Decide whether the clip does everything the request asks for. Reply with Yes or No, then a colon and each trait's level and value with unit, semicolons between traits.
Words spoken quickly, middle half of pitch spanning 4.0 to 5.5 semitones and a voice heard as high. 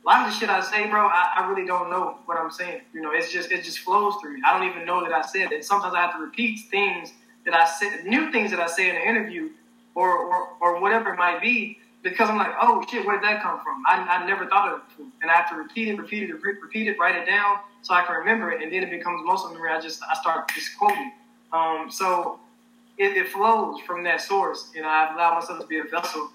Yes: fast, 280 wpm; average, 4.8 semitones; high, 200 Hz